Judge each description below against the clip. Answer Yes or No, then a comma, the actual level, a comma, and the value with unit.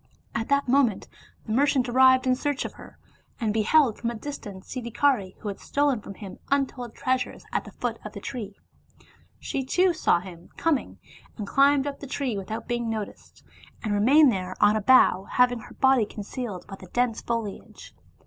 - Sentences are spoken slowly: No, average, 185 wpm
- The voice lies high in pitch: Yes, high, 240 Hz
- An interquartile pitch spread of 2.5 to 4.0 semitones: No, average, 4.6 semitones